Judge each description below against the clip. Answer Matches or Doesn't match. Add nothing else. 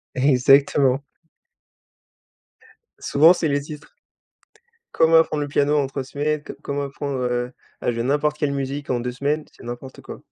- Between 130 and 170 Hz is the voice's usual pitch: Matches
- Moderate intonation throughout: Doesn't match